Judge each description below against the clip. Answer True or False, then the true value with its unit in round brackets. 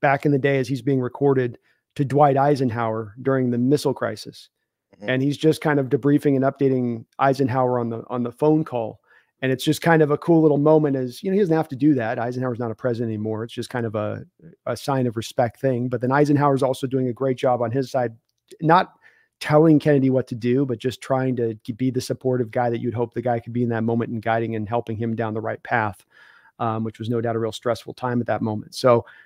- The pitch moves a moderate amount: True (3.2 semitones)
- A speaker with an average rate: False (250 wpm)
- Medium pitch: False (125 Hz)